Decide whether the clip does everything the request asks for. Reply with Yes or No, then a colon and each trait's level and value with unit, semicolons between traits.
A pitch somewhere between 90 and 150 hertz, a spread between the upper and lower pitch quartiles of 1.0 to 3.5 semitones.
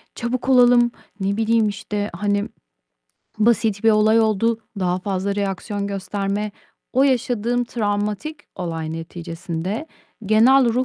No: high, 210 Hz; average, 3.2 semitones